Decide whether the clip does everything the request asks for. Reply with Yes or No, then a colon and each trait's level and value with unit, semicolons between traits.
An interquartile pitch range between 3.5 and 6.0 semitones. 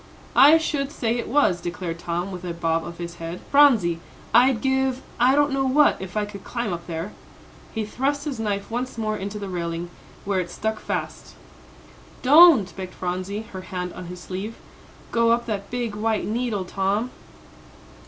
Yes: wide, 5.5 semitones